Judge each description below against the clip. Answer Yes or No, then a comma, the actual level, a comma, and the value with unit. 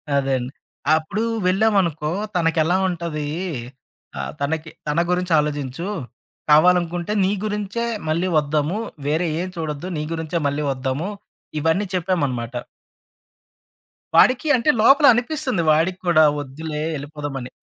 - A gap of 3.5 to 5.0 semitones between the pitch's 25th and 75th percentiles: Yes, average, 3.8 semitones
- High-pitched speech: No, medium, 160 Hz